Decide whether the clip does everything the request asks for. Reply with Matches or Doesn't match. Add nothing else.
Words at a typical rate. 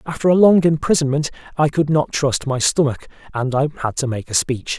Doesn't match